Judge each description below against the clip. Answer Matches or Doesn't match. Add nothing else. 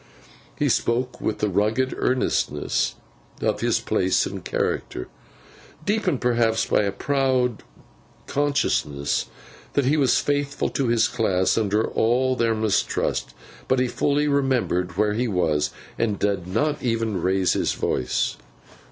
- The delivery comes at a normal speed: Doesn't match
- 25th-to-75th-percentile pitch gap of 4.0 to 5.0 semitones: Matches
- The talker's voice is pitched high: Doesn't match